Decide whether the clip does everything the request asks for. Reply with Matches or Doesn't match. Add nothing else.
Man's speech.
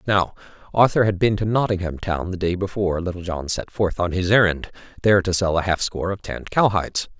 Matches